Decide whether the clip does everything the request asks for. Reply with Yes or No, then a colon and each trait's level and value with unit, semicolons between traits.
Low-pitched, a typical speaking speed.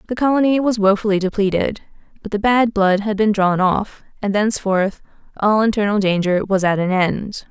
No: high, 205 Hz; average, 175 wpm